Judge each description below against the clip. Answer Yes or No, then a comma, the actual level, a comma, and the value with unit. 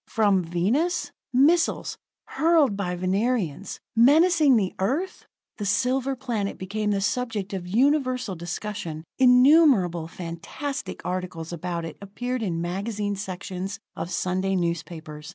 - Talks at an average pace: No, slow, 115 wpm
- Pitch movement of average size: No, wide, 6.0 semitones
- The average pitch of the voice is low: No, high, 200 Hz